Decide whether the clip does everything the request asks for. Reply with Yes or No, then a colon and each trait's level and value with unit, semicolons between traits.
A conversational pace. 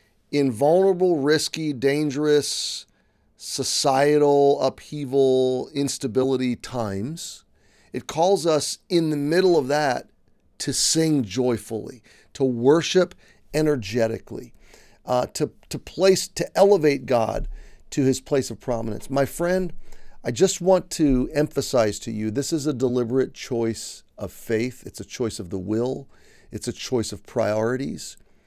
No: slow, 130 wpm